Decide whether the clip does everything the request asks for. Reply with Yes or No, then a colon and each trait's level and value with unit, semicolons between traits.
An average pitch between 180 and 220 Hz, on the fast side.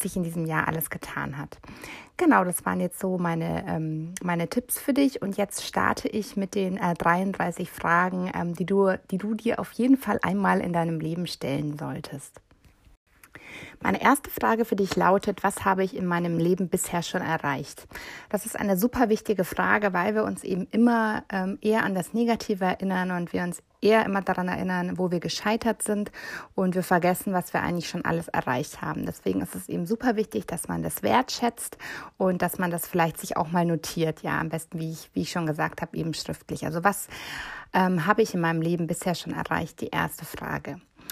Yes: medium, 185 Hz; fast, 195 wpm